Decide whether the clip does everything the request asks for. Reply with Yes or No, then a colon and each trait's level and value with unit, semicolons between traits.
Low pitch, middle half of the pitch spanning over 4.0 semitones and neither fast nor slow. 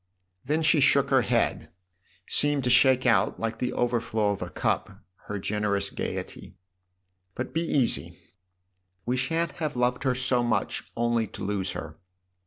Yes: low, 120 Hz; average, 4.4 semitones; average, 165 wpm